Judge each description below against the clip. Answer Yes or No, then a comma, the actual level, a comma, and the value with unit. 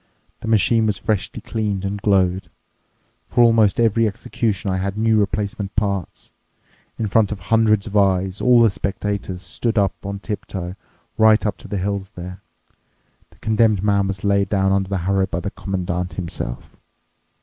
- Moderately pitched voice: No, low, 100 Hz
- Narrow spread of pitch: Yes, narrow, 2.2 semitones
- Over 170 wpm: No, average, 160 wpm